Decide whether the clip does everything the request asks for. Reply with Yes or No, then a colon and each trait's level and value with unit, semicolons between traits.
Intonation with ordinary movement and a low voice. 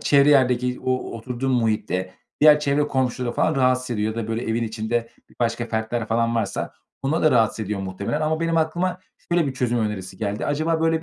Yes: average, 4.8 semitones; low, 120 Hz